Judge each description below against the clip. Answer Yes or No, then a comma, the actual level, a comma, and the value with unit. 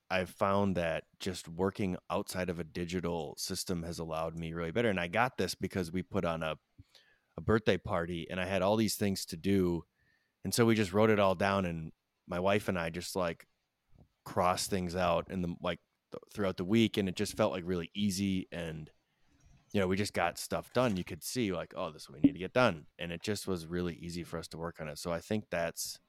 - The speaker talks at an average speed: No, fast, 235 wpm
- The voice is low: Yes, very low, 90 Hz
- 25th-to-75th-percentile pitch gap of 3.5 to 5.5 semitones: No, narrow, 2.6 semitones